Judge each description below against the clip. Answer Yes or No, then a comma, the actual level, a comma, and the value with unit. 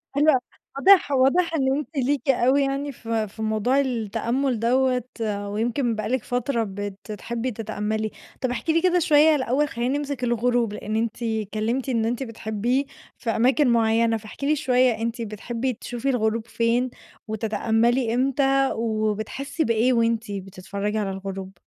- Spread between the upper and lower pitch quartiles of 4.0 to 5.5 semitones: No, average, 3.5 semitones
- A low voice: No, high, 235 Hz